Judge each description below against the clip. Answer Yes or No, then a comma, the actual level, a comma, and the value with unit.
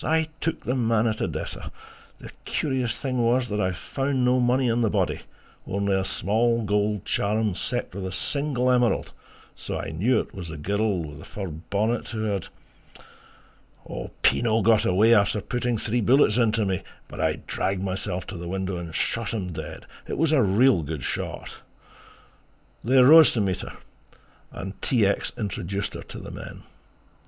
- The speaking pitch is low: Yes, low, 110 Hz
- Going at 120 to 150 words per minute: No, average, 180 wpm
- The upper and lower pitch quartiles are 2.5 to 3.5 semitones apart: No, average, 4.2 semitones